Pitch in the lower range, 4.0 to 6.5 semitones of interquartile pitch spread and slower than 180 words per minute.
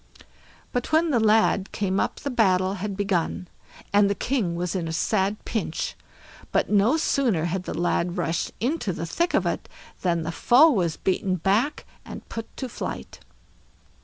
No: high, 200 Hz; average, 4.8 semitones; average, 170 wpm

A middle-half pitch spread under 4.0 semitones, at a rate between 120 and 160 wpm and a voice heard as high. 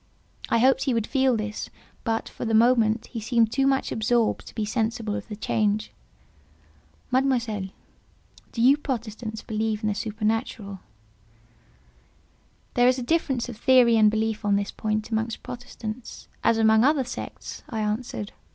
Yes: narrow, 2.4 semitones; average, 155 wpm; high, 225 Hz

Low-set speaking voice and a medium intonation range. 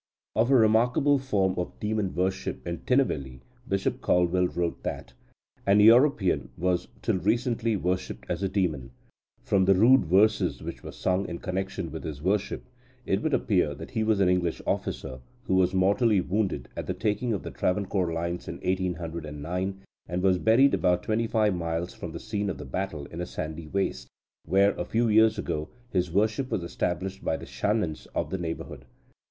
Yes: very low, 95 Hz; average, 3.6 semitones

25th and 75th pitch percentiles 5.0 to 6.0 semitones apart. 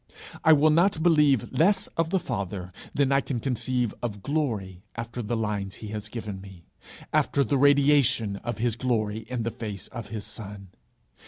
Yes: wide, 5.4 semitones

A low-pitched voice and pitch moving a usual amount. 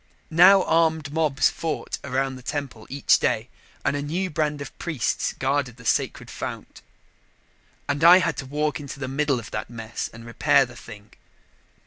No: medium, 145 Hz; average, 3.6 semitones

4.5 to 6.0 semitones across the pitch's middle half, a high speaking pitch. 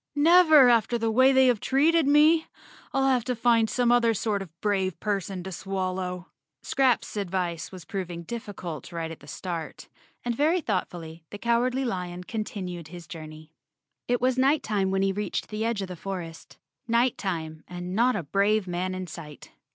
Yes: wide, 5.4 semitones; high, 200 Hz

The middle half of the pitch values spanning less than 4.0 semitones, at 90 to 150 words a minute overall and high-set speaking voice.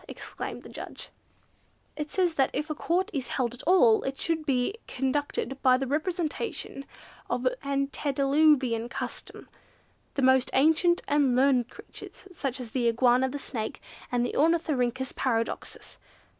Yes: average, 3.4 semitones; average, 140 wpm; very high, 275 Hz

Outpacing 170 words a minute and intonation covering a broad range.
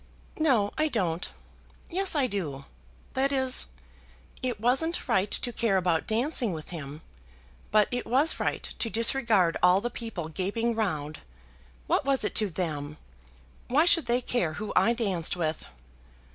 No: average, 150 wpm; wide, 6.2 semitones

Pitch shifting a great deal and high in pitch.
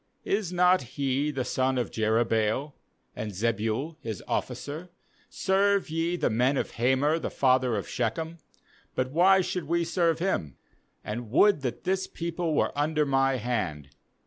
No: wide, 6.1 semitones; medium, 140 Hz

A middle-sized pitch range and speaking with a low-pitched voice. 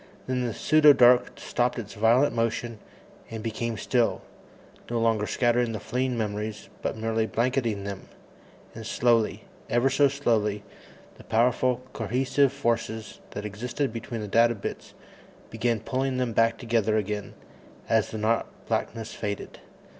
No: narrow, 2.2 semitones; low, 115 Hz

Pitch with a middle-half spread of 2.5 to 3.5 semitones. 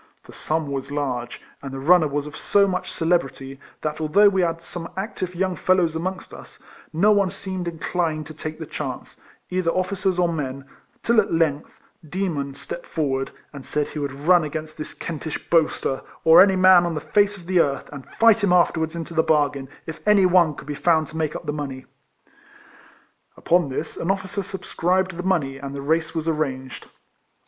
No: average, 3.9 semitones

